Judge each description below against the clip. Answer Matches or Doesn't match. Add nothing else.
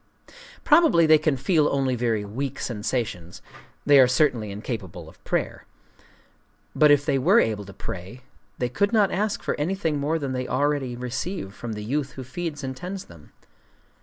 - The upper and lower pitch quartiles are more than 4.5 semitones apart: Matches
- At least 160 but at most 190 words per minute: Matches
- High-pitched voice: Doesn't match